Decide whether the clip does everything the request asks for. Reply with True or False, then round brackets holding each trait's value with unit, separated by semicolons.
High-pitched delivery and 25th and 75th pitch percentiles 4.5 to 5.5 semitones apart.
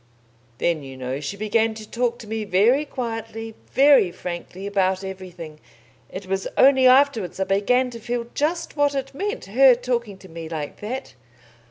True (220 Hz; 5.2 semitones)